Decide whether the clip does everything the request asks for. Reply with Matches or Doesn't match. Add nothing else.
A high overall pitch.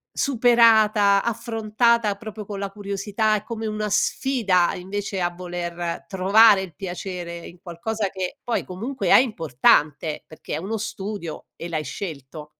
Matches